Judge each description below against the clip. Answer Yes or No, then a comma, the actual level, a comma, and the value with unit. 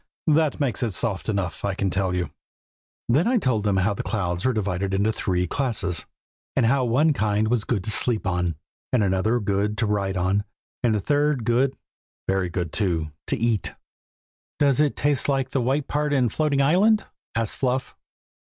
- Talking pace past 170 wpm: Yes, average, 185 wpm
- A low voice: Yes, low, 110 Hz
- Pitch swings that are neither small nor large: No, wide, 5.8 semitones